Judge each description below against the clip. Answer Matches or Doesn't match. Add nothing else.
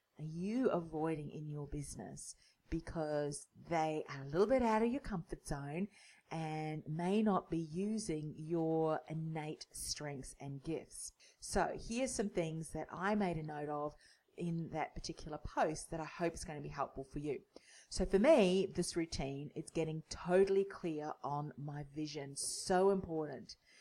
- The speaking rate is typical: Matches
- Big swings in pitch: Doesn't match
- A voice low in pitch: Doesn't match